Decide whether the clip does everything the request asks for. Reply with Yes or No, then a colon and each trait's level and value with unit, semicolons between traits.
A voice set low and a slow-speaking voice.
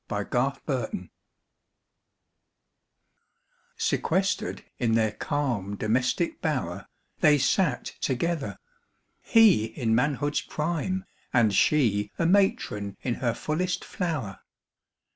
Yes: low, 130 Hz; slow, 95 wpm